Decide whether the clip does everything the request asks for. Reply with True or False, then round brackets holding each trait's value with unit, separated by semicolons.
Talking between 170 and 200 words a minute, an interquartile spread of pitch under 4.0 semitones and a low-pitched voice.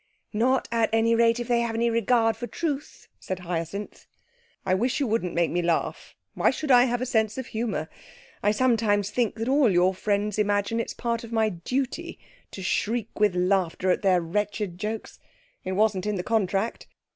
False (190 wpm; 3.5 semitones; 220 Hz)